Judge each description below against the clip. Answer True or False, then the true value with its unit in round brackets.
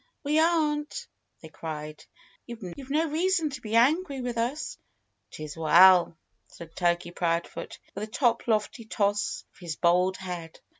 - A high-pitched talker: True (215 Hz)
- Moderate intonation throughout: False (8.8 semitones)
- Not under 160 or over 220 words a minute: False (140 wpm)